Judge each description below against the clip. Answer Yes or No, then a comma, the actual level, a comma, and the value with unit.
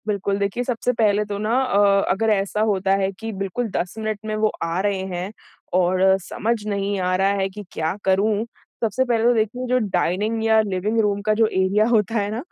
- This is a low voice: No, high, 205 Hz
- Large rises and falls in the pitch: No, narrow, 2.4 semitones